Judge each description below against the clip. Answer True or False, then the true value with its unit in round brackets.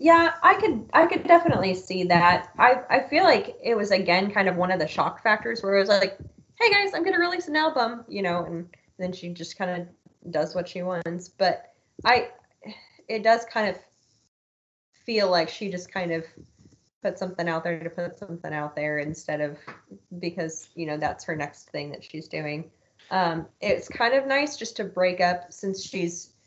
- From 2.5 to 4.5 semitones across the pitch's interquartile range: False (5.3 semitones)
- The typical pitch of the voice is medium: True (180 Hz)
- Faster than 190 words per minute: True (205 wpm)